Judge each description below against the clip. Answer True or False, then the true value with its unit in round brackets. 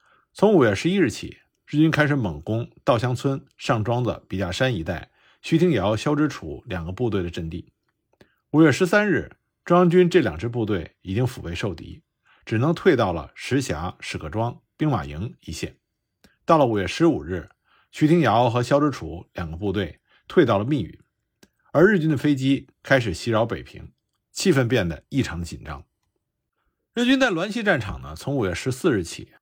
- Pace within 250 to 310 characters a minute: True (265 characters per minute)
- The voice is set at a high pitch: False (120 Hz)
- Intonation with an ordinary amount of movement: False (7.9 semitones)